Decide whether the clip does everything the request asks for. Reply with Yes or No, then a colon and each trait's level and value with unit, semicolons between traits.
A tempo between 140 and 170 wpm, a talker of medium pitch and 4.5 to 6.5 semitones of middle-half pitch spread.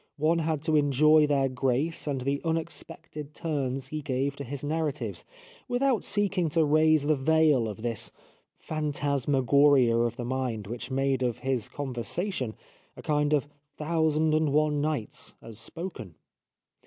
No: average, 155 wpm; medium, 145 Hz; average, 3.2 semitones